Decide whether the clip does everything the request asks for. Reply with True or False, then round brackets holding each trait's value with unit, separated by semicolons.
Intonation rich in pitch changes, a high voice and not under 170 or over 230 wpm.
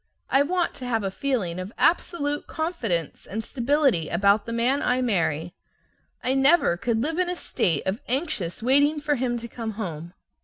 True (6.7 semitones; 240 Hz; 180 wpm)